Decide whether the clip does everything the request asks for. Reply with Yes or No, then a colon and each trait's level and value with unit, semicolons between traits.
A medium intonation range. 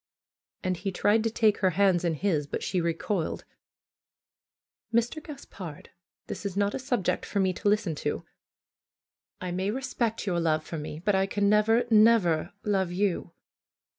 Yes: average, 3.6 semitones